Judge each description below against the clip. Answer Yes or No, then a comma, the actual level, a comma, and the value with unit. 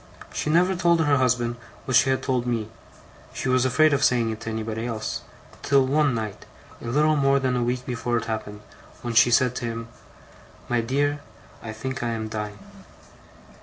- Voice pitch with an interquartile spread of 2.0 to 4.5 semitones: Yes, average, 3.1 semitones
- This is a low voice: Yes, low, 125 Hz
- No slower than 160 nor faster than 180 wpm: No, average, 190 wpm